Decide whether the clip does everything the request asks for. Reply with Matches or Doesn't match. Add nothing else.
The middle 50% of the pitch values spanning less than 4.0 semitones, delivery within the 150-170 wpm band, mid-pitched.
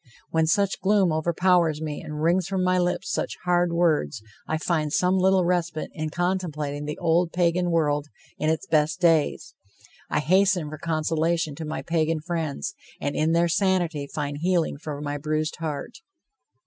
Matches